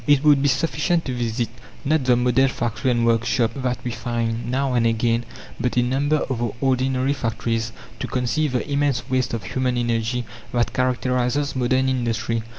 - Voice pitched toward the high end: No, low, 125 Hz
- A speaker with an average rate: Yes, average, 175 wpm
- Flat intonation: Yes, narrow, 2.1 semitones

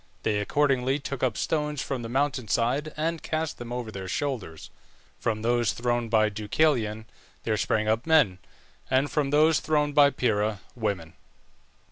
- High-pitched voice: No, low, 120 Hz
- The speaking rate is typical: Yes, average, 155 wpm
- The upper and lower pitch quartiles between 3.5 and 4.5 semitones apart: No, average, 5.1 semitones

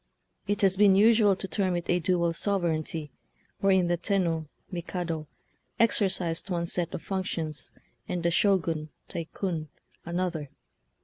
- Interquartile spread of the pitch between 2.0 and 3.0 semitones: Yes, average, 2.7 semitones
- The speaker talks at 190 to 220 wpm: No, slow, 135 wpm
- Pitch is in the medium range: Yes, medium, 175 Hz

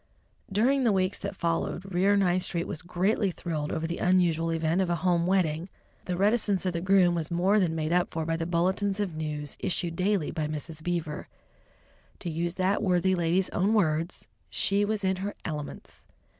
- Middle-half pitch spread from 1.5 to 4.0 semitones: Yes, average, 2.8 semitones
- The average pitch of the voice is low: No, medium, 180 Hz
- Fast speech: No, average, 190 wpm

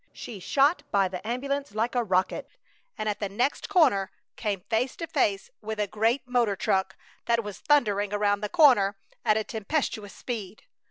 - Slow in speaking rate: No, average, 175 wpm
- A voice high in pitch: Yes, high, 215 Hz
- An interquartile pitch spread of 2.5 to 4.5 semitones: Yes, average, 3.8 semitones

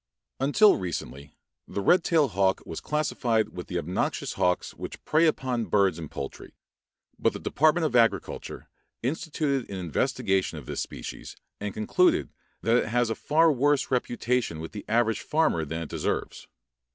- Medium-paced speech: Yes, average, 160 wpm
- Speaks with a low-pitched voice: Yes, low, 115 Hz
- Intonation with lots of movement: Yes, wide, 7.8 semitones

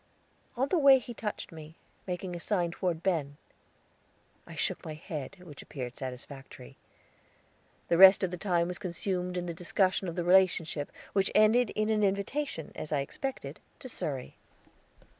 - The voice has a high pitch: No, medium, 180 Hz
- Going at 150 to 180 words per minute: Yes, average, 160 wpm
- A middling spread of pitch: Yes, average, 4.1 semitones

